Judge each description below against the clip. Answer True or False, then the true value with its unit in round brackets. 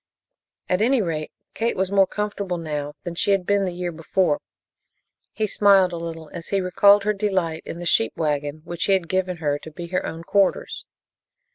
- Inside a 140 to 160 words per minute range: False (195 wpm)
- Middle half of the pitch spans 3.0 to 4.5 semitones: True (3.4 semitones)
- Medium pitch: True (180 Hz)